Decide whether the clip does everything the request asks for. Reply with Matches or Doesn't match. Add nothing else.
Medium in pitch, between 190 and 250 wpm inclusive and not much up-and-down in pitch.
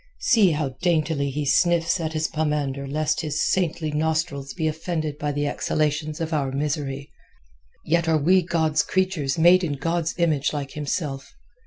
Doesn't match